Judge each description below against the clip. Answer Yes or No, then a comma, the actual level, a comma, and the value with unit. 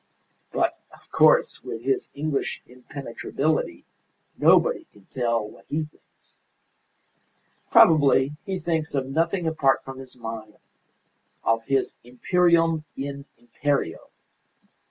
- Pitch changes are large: No, average, 4.5 semitones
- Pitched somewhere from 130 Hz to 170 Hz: Yes, medium, 140 Hz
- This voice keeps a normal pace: No, slow, 110 wpm